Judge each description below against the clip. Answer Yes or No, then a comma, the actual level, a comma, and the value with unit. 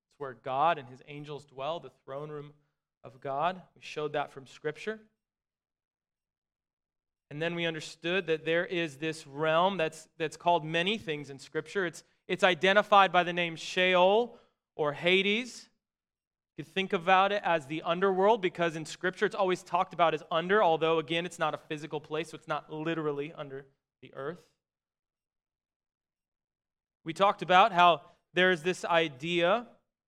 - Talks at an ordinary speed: Yes, average, 160 wpm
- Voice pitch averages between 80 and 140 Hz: No, medium, 165 Hz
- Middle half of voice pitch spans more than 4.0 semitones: No, average, 3.1 semitones